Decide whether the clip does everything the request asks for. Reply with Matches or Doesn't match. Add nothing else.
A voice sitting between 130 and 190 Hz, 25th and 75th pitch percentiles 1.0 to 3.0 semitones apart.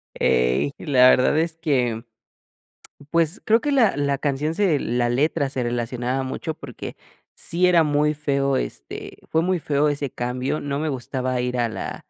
Doesn't match